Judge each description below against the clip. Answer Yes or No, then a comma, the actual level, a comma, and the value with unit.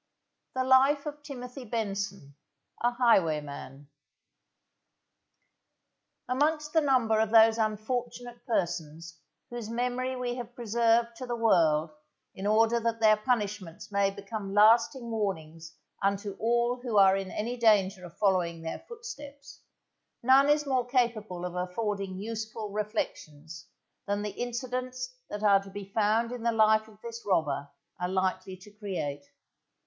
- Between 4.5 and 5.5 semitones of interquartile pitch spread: No, average, 4.0 semitones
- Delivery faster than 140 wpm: No, slow, 135 wpm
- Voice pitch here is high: Yes, high, 220 Hz